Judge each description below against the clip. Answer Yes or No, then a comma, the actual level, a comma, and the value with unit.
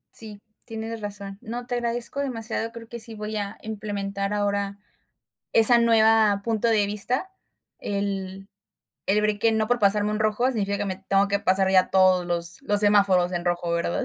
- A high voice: Yes, high, 205 Hz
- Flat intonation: Yes, narrow, 2.2 semitones